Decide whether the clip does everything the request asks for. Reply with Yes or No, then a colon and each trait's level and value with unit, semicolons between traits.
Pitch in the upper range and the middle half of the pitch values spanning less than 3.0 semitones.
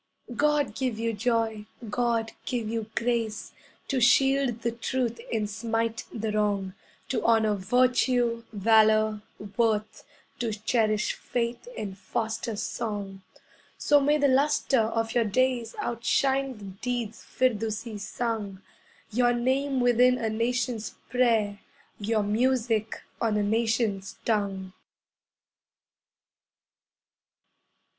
Yes: high, 230 Hz; narrow, 2.4 semitones